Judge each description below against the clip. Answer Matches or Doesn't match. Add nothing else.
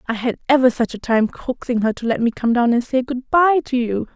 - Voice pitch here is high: Matches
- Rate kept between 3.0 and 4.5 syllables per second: Doesn't match